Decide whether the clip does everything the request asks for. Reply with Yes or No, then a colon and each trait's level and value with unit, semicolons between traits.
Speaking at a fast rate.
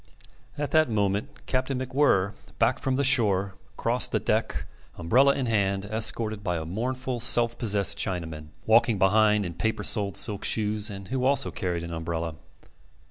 No: average, 160 wpm